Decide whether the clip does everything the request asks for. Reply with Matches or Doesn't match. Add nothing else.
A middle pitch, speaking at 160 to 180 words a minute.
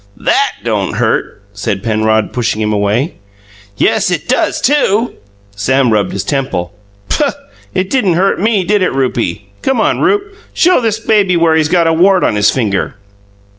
Matches